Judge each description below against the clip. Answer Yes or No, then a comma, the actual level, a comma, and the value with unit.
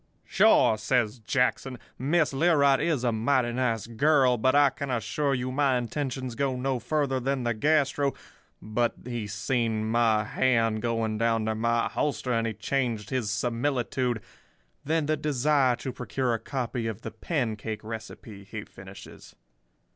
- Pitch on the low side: Yes, low, 125 Hz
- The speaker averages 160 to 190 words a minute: No, average, 150 wpm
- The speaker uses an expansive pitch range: No, average, 3.3 semitones